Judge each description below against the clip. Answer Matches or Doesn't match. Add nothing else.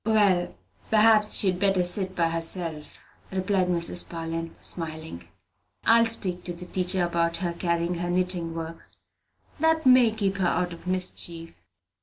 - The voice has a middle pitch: Matches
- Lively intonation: Doesn't match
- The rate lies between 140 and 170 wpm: Matches